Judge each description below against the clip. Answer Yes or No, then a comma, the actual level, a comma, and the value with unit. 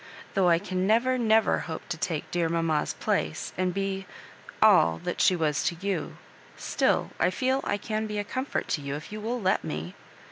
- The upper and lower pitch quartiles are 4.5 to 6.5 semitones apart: Yes, average, 4.9 semitones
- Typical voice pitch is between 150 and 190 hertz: Yes, medium, 185 Hz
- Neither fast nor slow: No, fast, 210 wpm